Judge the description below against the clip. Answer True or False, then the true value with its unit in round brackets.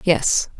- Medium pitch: True (175 Hz)